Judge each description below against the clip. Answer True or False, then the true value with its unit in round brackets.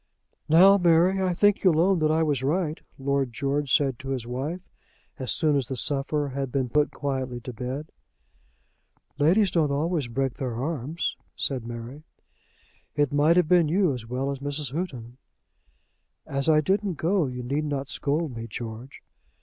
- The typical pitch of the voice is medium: True (145 Hz)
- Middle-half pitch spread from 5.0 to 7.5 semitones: False (3.8 semitones)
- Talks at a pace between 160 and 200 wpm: True (170 wpm)